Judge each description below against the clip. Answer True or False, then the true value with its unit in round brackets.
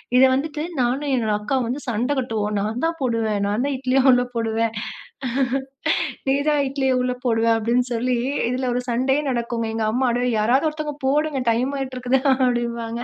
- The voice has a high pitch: True (250 Hz)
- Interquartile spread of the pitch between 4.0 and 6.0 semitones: False (2.6 semitones)